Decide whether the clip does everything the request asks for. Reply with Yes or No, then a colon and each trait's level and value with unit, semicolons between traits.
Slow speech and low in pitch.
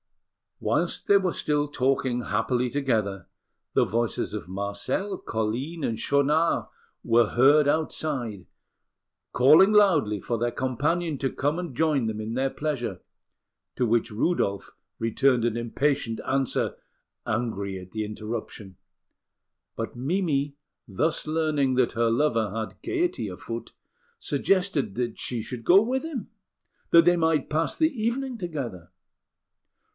Yes: slow, 130 wpm; low, 130 Hz